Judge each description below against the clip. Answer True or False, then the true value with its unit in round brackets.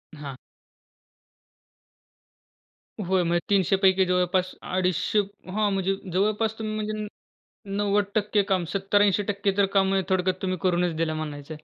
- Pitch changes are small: True (2.2 semitones)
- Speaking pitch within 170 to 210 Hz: True (190 Hz)